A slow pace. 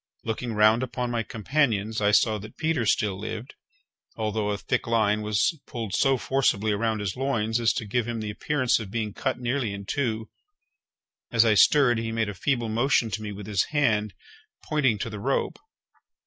No: average, 190 wpm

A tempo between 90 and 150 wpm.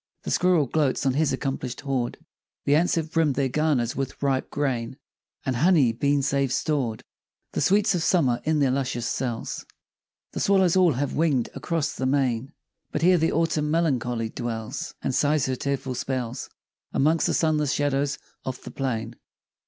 No: average, 170 wpm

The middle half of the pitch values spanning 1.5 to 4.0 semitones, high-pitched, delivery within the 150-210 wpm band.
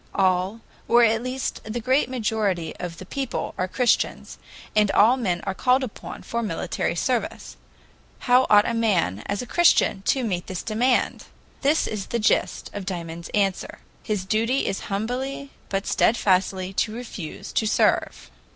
No: average, 4.5 semitones; high, 215 Hz; average, 160 wpm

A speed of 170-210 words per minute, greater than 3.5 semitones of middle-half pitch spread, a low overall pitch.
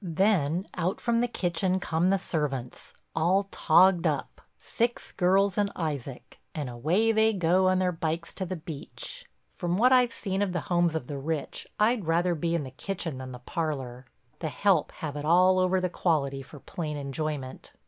No: average, 180 wpm; average, 4.2 semitones; medium, 170 Hz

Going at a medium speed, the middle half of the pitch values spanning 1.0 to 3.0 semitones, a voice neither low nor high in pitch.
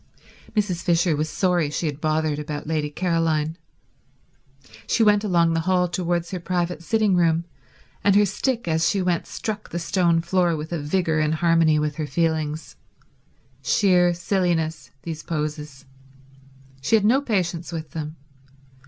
Yes: average, 155 wpm; narrow, 2.6 semitones; medium, 170 Hz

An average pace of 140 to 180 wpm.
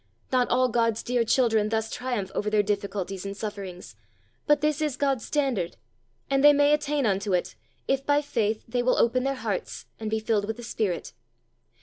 No: average, 190 wpm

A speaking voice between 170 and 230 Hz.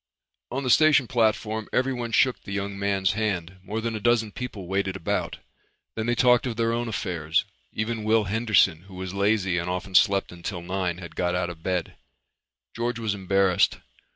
No: low, 100 Hz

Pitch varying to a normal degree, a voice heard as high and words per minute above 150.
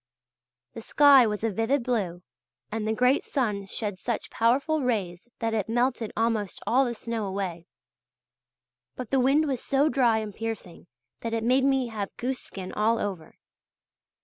Yes: average, 3.5 semitones; high, 225 Hz; average, 165 wpm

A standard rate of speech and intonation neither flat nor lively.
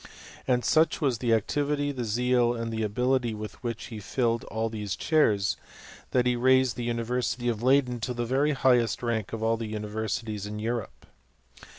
No: average, 185 wpm; narrow, 2.3 semitones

